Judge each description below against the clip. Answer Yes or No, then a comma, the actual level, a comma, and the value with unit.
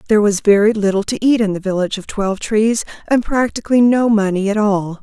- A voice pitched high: Yes, high, 210 Hz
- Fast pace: Yes, fast, 215 wpm